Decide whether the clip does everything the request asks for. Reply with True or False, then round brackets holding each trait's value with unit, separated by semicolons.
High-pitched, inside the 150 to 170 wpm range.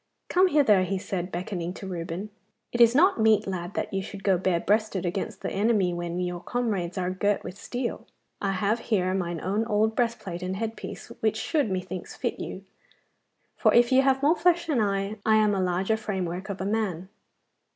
False (200 Hz; 200 wpm)